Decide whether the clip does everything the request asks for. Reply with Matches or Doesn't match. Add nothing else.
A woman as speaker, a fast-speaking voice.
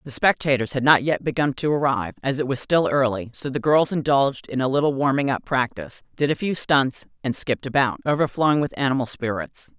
Matches